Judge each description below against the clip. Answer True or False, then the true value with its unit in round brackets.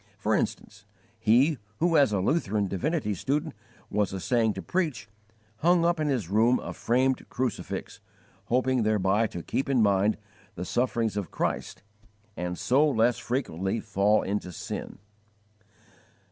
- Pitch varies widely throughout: False (4.8 semitones)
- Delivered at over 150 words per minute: False (140 wpm)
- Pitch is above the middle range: False (115 Hz)